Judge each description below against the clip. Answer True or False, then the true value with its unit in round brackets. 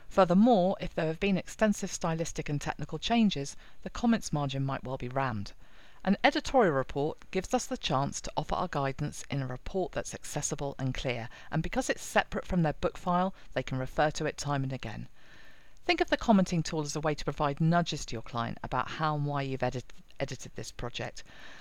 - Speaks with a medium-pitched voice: True (155 Hz)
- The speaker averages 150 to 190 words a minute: False (205 wpm)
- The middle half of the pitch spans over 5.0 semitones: True (5.5 semitones)